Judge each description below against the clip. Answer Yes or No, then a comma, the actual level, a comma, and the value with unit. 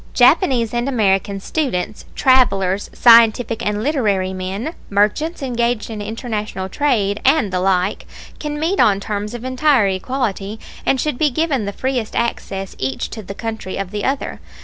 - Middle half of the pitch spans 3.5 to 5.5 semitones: Yes, average, 4.7 semitones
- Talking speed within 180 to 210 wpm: No, average, 155 wpm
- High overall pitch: Yes, high, 220 Hz